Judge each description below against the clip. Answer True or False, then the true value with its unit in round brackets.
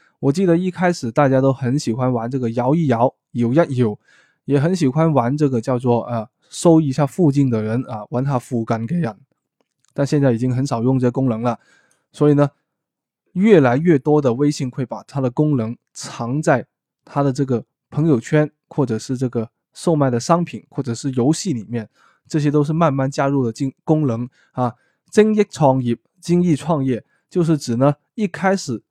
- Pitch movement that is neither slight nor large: True (4.3 semitones)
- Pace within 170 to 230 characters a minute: False (265 characters per minute)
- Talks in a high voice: False (140 Hz)